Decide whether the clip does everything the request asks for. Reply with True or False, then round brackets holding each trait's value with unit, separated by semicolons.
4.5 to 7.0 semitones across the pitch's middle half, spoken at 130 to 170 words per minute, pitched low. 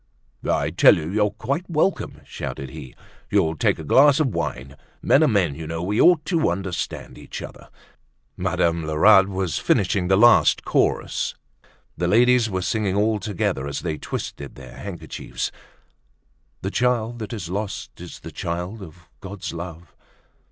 True (5.1 semitones; 160 wpm; 95 Hz)